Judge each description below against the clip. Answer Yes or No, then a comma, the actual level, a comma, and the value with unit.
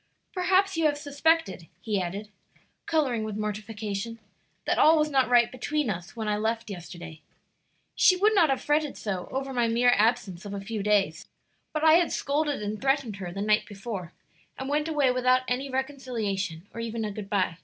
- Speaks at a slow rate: No, average, 185 wpm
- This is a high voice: Yes, high, 230 Hz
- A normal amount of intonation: No, wide, 5.8 semitones